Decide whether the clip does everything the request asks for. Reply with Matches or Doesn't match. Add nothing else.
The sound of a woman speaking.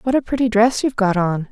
Matches